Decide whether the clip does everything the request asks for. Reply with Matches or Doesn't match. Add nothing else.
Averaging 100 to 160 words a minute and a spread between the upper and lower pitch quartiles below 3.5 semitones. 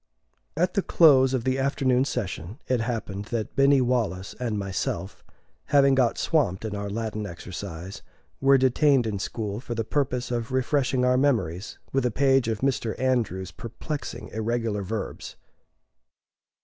Doesn't match